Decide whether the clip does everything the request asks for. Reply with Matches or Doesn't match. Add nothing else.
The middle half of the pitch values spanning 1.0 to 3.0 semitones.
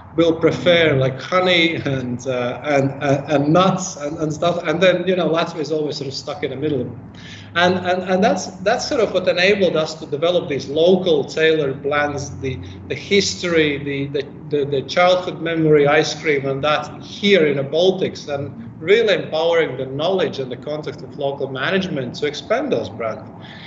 Doesn't match